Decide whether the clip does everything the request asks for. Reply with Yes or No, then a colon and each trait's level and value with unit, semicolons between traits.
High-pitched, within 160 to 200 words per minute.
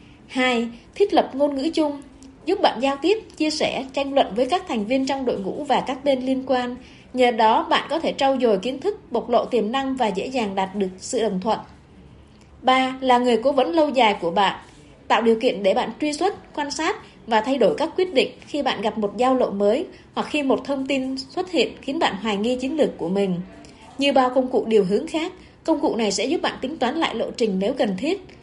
No: very high, 260 Hz; average, 240 wpm